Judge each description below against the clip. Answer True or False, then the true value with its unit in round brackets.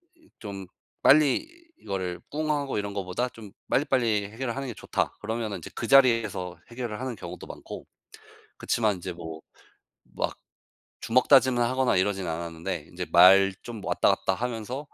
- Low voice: True (110 Hz)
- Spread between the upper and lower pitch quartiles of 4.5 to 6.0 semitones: True (5.4 semitones)